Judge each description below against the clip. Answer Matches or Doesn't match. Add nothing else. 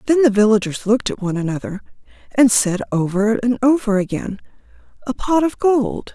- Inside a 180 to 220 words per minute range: Doesn't match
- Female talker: Matches